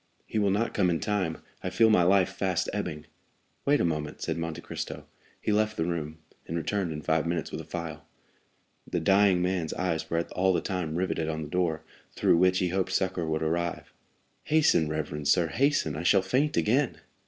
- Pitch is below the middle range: Yes, very low, 90 Hz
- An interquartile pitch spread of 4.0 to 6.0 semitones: No, average, 3.5 semitones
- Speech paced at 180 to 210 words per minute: Yes, average, 200 wpm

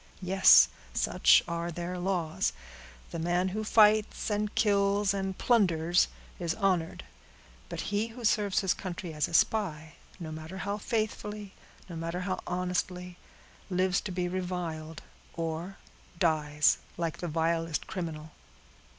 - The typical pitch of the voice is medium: Yes, medium, 180 Hz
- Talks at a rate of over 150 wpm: No, slow, 135 wpm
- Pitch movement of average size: Yes, average, 3.2 semitones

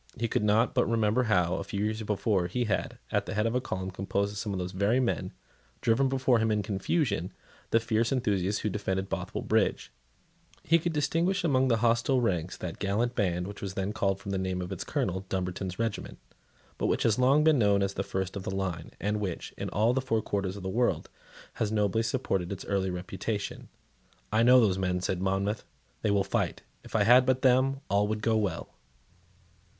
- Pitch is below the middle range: Yes, low, 105 Hz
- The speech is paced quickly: Yes, fast, 210 wpm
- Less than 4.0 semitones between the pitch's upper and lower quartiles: Yes, average, 3.4 semitones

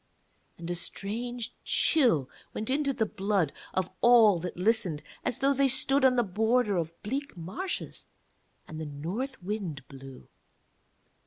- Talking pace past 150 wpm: No, average, 145 wpm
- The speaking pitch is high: Yes, high, 215 Hz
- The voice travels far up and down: Yes, wide, 6.8 semitones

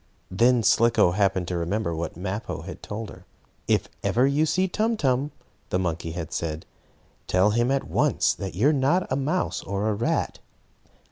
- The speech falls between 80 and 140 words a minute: No, average, 180 wpm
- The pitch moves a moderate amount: No, wide, 6.9 semitones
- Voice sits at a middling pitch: No, low, 105 Hz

